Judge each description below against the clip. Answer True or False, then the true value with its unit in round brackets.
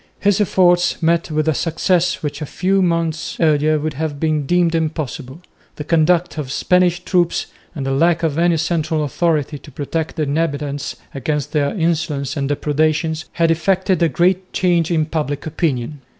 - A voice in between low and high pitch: True (160 Hz)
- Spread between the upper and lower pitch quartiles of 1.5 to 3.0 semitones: True (2.5 semitones)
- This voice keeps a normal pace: True (170 wpm)